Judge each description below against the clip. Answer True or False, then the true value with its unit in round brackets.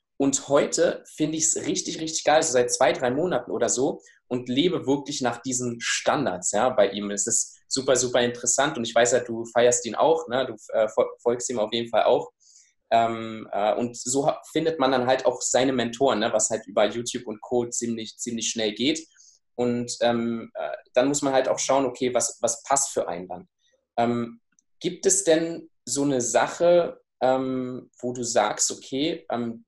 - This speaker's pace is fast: True (200 wpm)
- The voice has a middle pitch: False (125 Hz)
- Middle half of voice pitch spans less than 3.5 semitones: True (2.8 semitones)